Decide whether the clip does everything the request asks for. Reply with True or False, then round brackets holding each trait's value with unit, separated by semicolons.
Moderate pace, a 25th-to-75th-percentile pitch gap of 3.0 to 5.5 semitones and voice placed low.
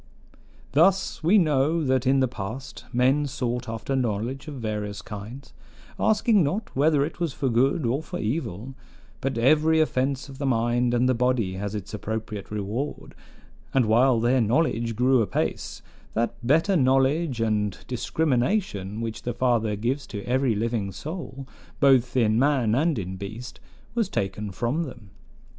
True (155 wpm; 4.0 semitones; 125 Hz)